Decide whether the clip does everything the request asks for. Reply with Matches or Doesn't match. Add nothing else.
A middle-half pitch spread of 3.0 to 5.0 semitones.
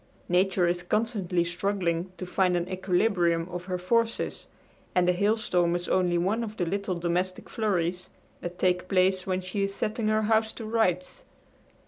Doesn't match